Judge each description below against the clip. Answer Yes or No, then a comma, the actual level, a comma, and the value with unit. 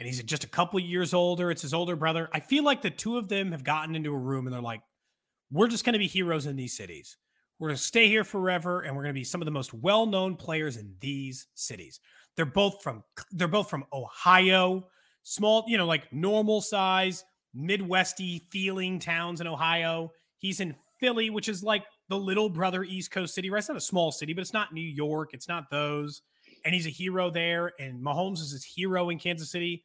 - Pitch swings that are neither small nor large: Yes, average, 3.9 semitones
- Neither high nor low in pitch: Yes, medium, 175 Hz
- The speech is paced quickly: Yes, fast, 220 wpm